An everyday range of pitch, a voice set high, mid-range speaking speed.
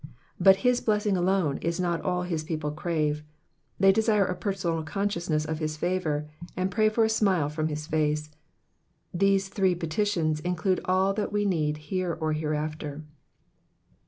No: average, 4.0 semitones; medium, 175 Hz; average, 160 wpm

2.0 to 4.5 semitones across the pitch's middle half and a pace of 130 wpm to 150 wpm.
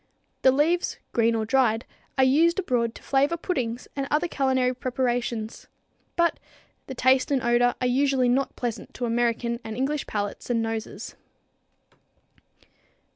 Yes: average, 2.7 semitones; average, 140 wpm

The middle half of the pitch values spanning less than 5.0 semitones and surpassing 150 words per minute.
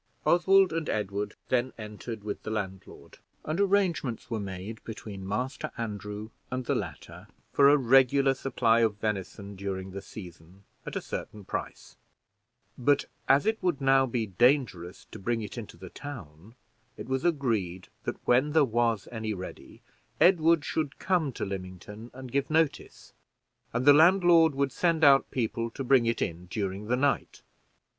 No: wide, 5.5 semitones; average, 160 wpm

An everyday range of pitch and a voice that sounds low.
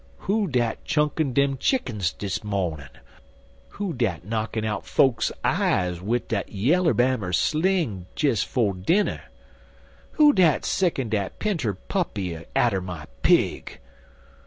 No: wide, 8.3 semitones; low, 120 Hz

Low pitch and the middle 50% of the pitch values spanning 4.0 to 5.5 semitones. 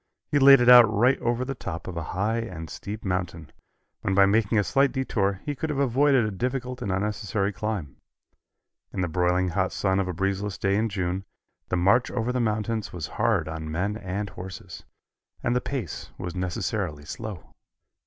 Yes: low, 100 Hz; average, 4.5 semitones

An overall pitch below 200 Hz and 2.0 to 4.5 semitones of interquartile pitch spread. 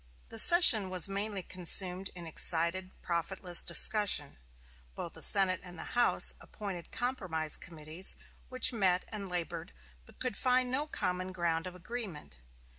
Yes: medium, 185 Hz; average, 3.8 semitones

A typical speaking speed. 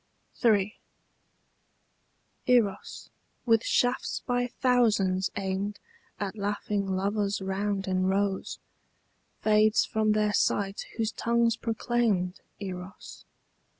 No: slow, 90 wpm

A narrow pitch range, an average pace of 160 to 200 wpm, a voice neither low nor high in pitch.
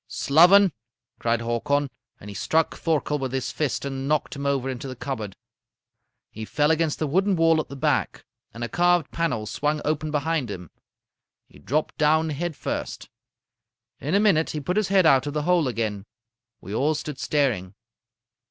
No: average, 4.1 semitones; average, 180 wpm; medium, 145 Hz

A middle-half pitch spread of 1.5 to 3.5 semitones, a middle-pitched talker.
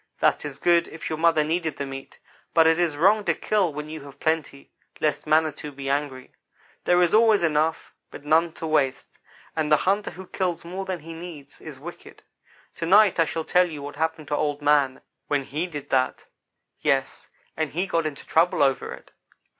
Yes: average, 2.8 semitones; medium, 160 Hz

